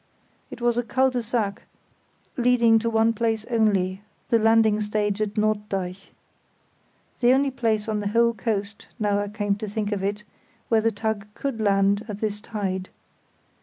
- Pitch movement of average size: No, narrow, 2.0 semitones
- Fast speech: No, average, 165 wpm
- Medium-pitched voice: No, high, 215 Hz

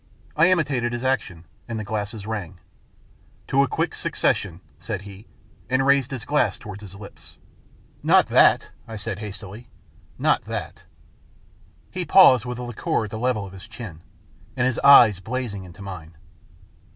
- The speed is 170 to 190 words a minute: Yes, average, 175 wpm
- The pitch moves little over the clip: No, average, 4.4 semitones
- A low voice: Yes, low, 110 Hz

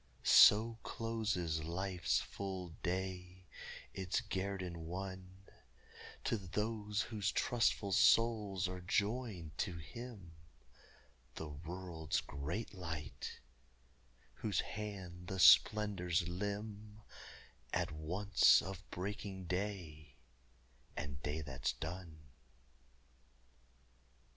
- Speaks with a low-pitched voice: Yes, very low, 95 Hz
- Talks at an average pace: No, slow, 85 wpm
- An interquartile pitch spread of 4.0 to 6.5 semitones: No, average, 3.3 semitones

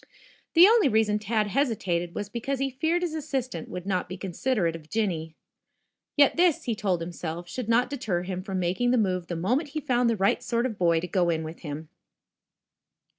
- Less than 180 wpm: No, fast, 205 wpm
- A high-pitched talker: Yes, high, 210 Hz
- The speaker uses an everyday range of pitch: No, wide, 6.4 semitones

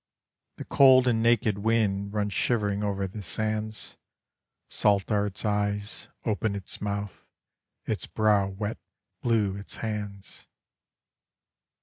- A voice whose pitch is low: Yes, low, 105 Hz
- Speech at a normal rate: No, slow, 115 wpm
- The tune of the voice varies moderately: No, narrow, 1.5 semitones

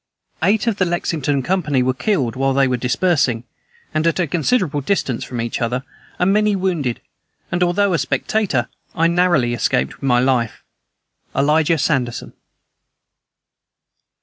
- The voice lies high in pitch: No, medium, 150 Hz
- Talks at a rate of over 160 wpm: No, average, 145 wpm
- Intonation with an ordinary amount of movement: No, wide, 6.0 semitones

